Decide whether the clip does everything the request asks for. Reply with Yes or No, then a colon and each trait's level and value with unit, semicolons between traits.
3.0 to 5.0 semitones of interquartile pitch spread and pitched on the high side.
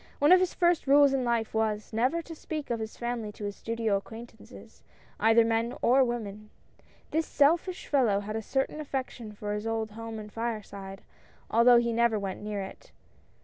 Yes: average, 3.9 semitones; high, 230 Hz